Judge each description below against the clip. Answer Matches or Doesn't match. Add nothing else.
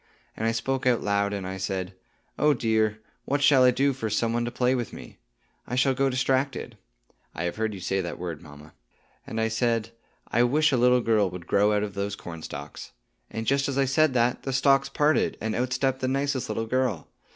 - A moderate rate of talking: Doesn't match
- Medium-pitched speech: Doesn't match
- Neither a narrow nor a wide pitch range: Matches